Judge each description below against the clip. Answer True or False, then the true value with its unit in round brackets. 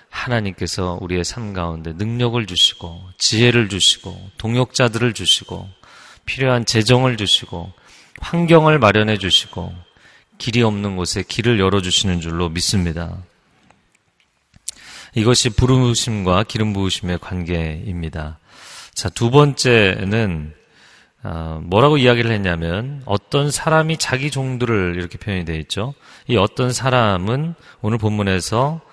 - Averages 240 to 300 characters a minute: True (275 characters per minute)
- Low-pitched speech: True (105 Hz)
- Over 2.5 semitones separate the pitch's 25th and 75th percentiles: True (5.4 semitones)